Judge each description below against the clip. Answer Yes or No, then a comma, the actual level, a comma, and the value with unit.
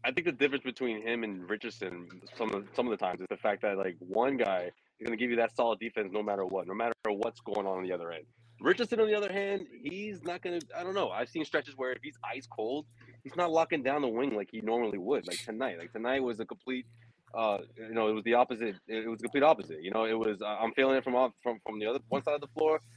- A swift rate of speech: Yes, fast, 285 wpm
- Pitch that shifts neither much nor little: Yes, average, 3.8 semitones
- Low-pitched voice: Yes, low, 120 Hz